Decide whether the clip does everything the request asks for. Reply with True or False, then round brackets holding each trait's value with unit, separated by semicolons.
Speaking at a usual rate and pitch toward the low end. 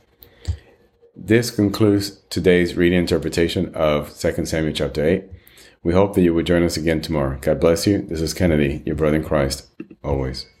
True (170 wpm; 85 Hz)